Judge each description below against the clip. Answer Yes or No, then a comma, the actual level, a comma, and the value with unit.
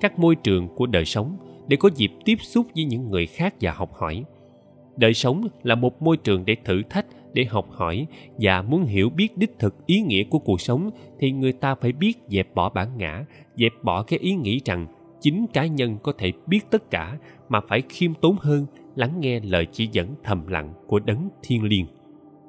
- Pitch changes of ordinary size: No, wide, 8.4 semitones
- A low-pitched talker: Yes, low, 125 Hz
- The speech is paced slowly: No, average, 215 wpm